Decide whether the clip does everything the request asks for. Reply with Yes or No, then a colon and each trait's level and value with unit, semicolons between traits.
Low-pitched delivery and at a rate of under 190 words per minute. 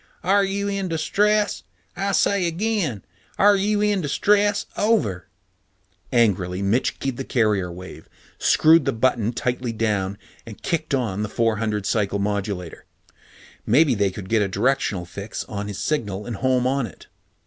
Yes: low, 120 Hz; average, 155 wpm